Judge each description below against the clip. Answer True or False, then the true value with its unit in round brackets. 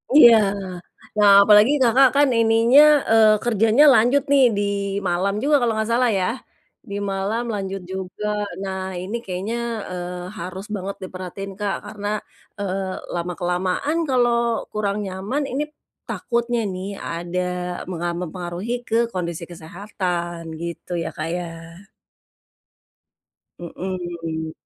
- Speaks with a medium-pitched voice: False (195 Hz)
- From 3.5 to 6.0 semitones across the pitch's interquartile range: True (4.0 semitones)